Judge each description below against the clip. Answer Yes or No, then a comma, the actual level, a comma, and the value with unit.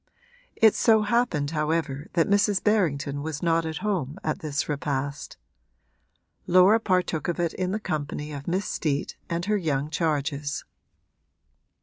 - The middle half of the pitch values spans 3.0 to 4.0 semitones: No, average, 4.4 semitones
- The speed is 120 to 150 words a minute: Yes, average, 140 wpm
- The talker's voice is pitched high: No, medium, 160 Hz